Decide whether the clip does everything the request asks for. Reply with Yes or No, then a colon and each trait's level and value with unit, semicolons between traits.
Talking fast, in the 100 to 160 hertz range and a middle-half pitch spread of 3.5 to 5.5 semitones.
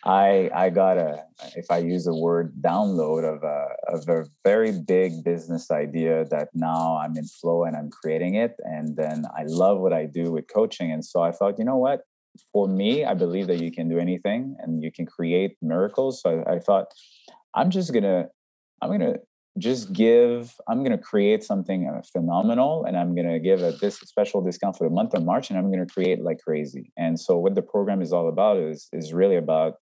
No: fast, 220 wpm; very low, 85 Hz; average, 4.0 semitones